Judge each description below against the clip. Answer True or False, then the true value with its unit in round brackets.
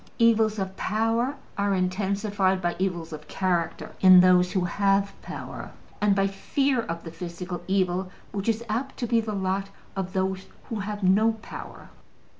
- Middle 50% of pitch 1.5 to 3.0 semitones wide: True (2.6 semitones)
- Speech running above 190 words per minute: False (165 wpm)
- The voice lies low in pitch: False (195 Hz)